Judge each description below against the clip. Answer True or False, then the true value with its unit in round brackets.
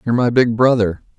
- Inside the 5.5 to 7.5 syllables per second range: True (6.5 syllables/s)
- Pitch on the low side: True (115 Hz)